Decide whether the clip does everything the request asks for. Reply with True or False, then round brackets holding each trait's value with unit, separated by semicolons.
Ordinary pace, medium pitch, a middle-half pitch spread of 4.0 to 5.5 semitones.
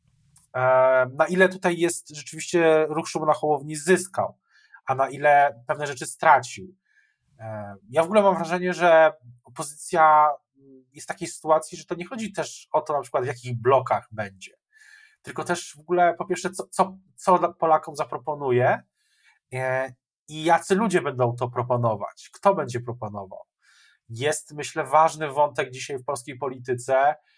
True (150 wpm; 150 Hz; 4.8 semitones)